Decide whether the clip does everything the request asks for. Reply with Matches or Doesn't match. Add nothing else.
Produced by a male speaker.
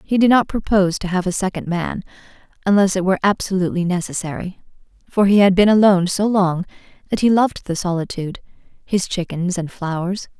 Doesn't match